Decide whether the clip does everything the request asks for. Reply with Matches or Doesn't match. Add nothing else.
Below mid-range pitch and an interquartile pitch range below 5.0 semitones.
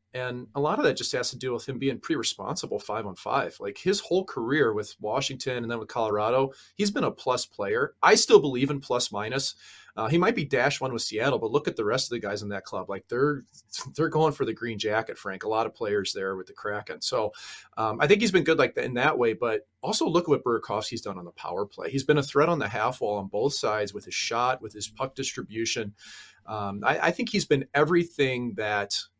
Doesn't match